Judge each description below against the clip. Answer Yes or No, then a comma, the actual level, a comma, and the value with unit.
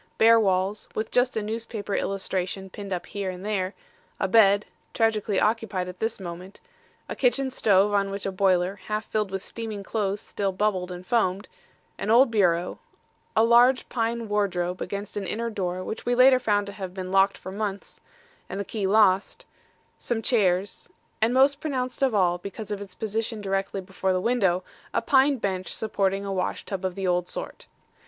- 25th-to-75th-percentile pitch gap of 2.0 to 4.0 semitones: Yes, average, 2.9 semitones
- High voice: Yes, high, 200 Hz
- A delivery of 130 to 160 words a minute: No, average, 185 wpm